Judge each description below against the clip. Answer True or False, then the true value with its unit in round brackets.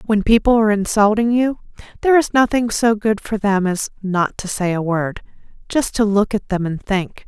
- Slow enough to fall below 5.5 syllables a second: True (5.0 syllables/s)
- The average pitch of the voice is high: True (210 Hz)